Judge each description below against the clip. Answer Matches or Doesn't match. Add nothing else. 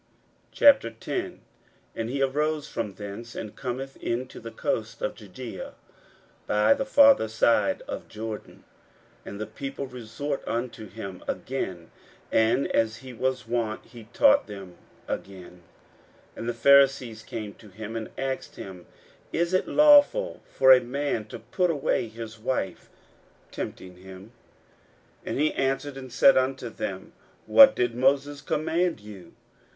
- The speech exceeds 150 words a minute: Doesn't match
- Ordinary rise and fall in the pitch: Matches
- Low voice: Matches